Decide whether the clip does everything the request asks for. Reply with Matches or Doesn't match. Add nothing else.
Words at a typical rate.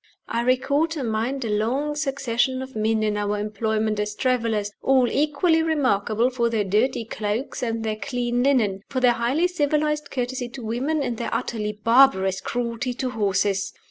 Matches